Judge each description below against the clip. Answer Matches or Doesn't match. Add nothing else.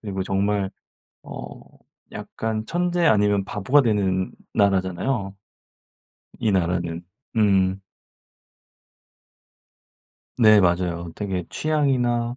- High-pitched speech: Doesn't match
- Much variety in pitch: Doesn't match